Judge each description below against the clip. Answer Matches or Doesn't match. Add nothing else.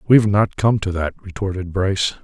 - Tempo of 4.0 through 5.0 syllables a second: Doesn't match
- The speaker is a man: Matches